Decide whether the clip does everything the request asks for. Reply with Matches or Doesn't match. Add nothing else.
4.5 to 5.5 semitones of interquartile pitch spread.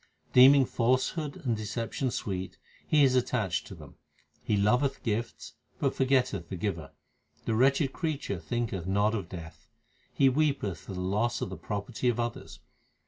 Matches